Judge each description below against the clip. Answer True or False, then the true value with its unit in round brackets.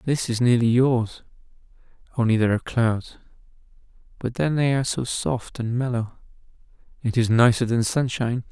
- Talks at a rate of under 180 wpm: True (150 wpm)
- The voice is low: True (120 Hz)